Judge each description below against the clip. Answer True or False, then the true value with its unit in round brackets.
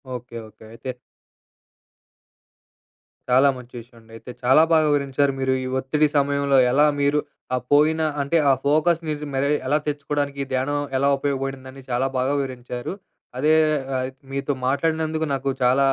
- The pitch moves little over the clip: True (2.1 semitones)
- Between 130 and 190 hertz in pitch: True (140 Hz)